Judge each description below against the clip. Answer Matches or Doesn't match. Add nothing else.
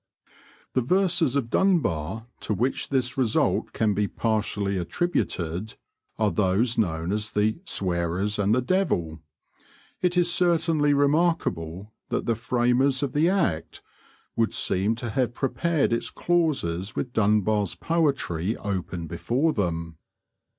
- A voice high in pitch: Doesn't match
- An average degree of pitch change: Doesn't match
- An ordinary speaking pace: Doesn't match